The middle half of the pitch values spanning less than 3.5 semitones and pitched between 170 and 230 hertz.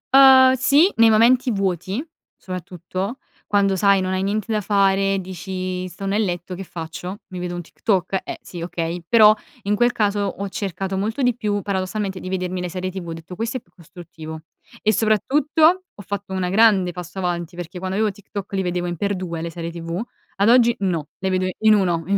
Yes: average, 2.9 semitones; high, 190 Hz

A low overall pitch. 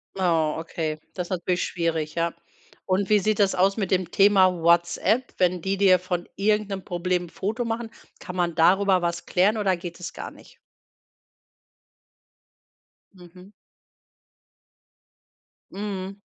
No: medium, 185 Hz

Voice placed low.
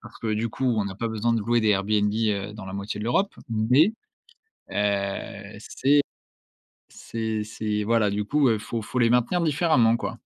Yes: low, 110 Hz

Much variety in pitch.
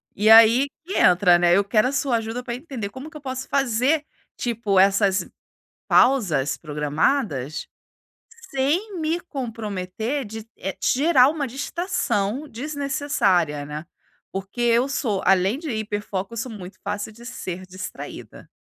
Yes: wide, 6.1 semitones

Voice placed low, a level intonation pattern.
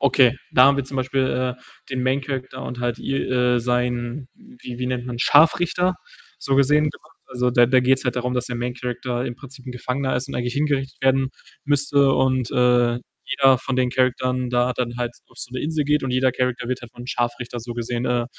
Yes: low, 125 Hz; narrow, 1.6 semitones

